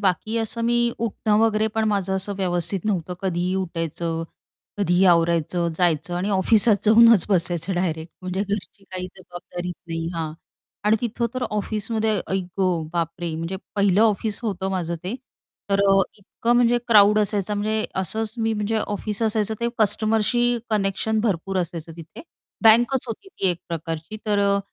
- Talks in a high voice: Yes, high, 200 Hz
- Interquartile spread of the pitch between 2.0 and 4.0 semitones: Yes, average, 3.6 semitones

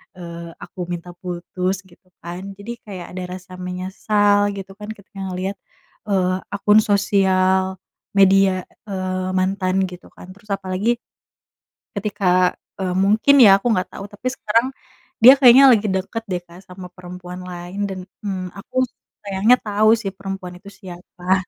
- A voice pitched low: No, high, 190 Hz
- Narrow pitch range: Yes, narrow, 1.9 semitones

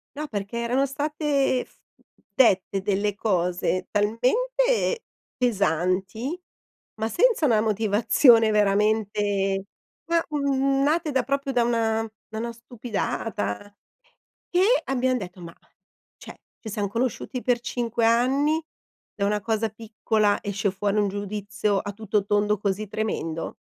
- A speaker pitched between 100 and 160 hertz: No, high, 220 Hz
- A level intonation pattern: No, average, 4.0 semitones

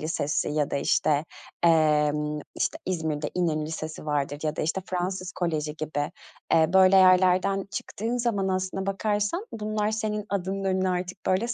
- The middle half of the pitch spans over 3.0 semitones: Yes, average, 4.0 semitones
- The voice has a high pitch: No, medium, 180 Hz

